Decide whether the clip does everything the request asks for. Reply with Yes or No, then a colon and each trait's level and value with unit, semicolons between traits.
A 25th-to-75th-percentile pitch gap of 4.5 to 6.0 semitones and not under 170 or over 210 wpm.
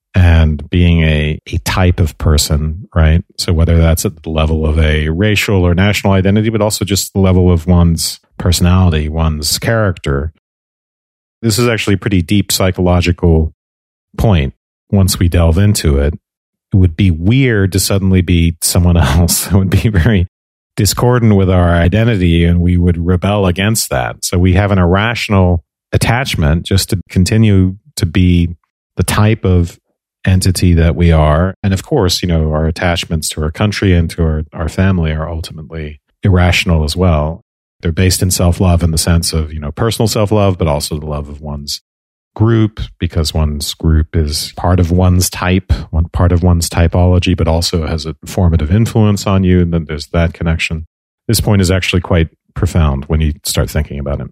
No: average, 3.3 semitones; average, 180 wpm